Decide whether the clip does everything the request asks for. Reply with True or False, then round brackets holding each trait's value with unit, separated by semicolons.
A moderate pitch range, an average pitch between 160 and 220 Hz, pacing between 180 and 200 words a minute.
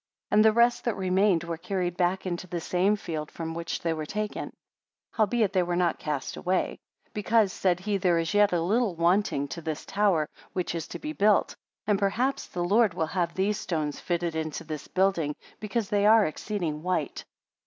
True (3.7 semitones; 185 Hz; 195 wpm)